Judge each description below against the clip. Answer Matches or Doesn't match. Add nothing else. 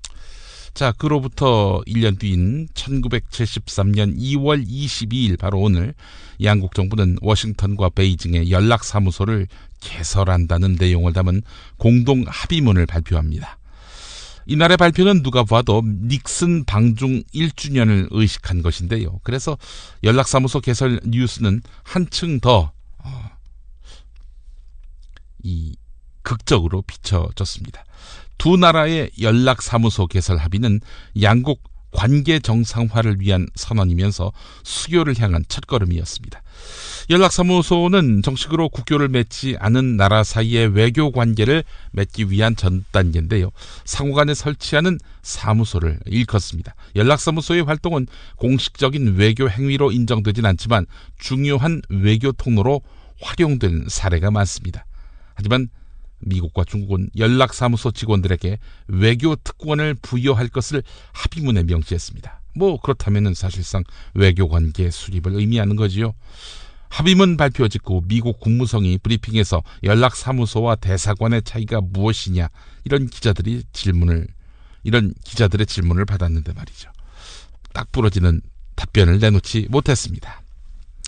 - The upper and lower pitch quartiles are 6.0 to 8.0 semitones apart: Doesn't match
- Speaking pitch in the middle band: Doesn't match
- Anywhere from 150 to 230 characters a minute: Doesn't match